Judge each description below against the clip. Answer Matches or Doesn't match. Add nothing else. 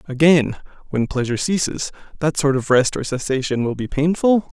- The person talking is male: Matches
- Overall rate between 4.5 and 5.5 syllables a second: Matches